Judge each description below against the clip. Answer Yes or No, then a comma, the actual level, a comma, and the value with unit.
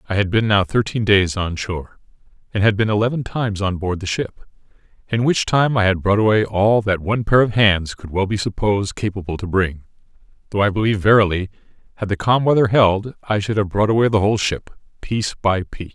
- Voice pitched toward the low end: Yes, low, 100 Hz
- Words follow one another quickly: Yes, fast, 215 wpm